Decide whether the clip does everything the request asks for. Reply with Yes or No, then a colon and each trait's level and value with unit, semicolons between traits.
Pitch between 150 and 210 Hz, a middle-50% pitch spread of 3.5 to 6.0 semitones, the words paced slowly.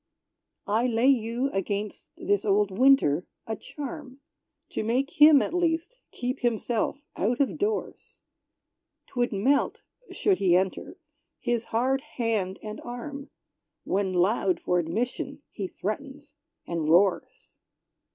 No: high, 235 Hz; wide, 5.6 semitones; slow, 120 wpm